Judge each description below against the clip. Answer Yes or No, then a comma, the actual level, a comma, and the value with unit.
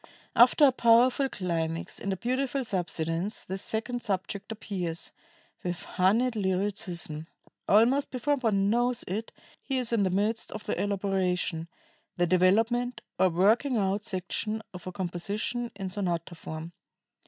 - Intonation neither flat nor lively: Yes, average, 4.4 semitones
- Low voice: No, high, 200 Hz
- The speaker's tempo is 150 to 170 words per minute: No, average, 140 wpm